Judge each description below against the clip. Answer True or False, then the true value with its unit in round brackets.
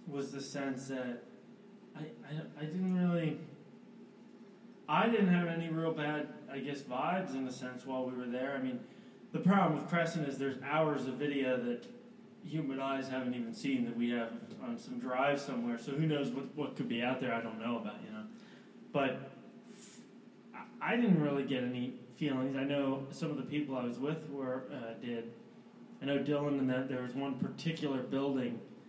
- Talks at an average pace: True (195 wpm)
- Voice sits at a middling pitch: True (145 Hz)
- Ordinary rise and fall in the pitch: False (6.9 semitones)